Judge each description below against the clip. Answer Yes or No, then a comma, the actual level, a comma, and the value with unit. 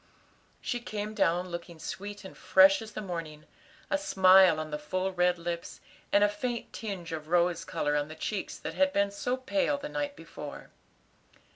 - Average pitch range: Yes, average, 4.1 semitones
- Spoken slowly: No, average, 180 wpm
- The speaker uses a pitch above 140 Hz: Yes, medium, 185 Hz